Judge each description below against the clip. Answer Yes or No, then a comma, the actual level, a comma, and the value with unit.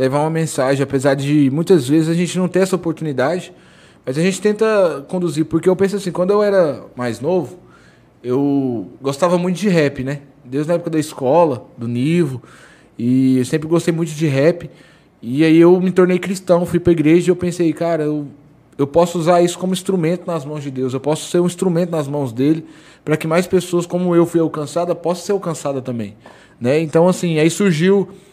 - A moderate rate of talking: No, fast, 205 wpm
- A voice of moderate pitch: Yes, medium, 165 Hz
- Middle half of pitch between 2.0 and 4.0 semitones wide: Yes, average, 3.6 semitones